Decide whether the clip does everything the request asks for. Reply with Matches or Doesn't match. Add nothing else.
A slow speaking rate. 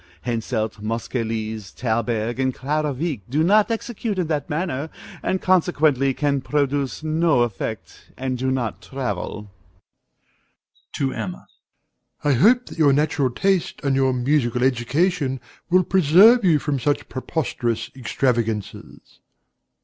Matches